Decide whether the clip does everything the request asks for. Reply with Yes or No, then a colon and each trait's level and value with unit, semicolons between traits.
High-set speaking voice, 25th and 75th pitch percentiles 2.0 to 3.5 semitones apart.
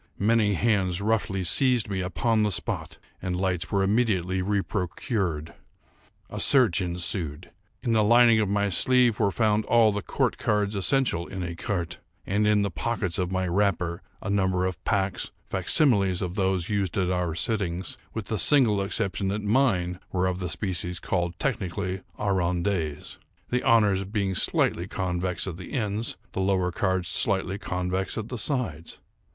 No: very low, 95 Hz; average, 2.8 semitones